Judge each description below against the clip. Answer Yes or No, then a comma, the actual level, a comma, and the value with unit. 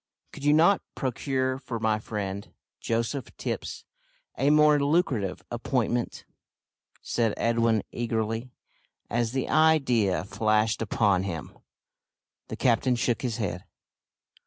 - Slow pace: Yes, slow, 110 wpm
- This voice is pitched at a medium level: No, low, 115 Hz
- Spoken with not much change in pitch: No, average, 3.6 semitones